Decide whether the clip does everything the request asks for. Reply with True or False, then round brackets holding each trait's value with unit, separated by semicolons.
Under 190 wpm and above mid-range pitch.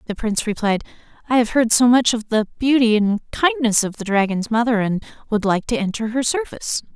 False (205 wpm; 230 Hz)